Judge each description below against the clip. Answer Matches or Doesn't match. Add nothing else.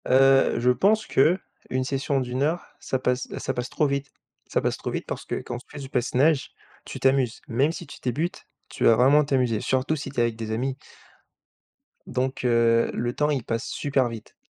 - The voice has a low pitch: Matches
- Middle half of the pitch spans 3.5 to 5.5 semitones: Doesn't match